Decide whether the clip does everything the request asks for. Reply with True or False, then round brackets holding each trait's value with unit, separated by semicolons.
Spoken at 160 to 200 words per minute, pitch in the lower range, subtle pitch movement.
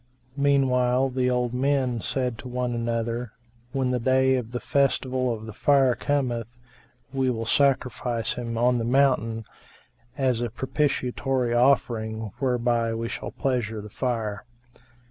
False (140 wpm; 125 Hz; 2.2 semitones)